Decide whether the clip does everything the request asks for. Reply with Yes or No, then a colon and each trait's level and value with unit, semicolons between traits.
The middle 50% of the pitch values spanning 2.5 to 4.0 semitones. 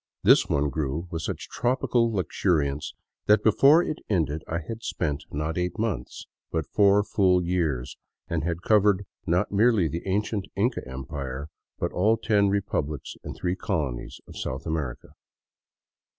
No: wide, 5.4 semitones